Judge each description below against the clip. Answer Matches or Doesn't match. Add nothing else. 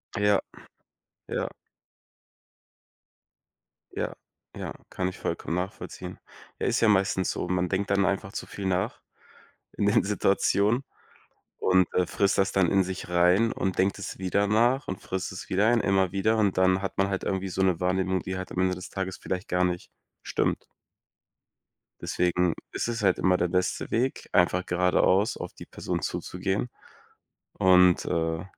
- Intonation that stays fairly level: Matches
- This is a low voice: Matches